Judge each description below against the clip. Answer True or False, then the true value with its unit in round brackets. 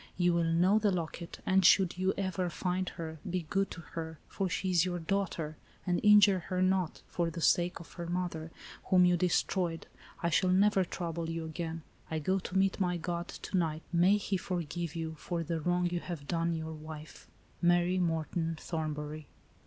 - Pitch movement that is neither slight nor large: False (2.1 semitones)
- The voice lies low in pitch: False (175 Hz)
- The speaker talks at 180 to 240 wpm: True (195 wpm)